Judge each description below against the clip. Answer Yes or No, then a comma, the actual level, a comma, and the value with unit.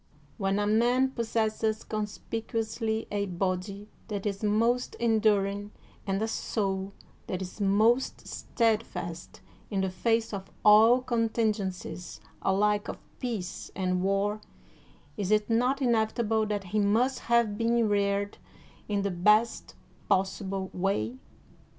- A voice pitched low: No, high, 210 Hz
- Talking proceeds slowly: Yes, slow, 125 wpm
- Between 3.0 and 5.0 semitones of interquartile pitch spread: No, narrow, 2.5 semitones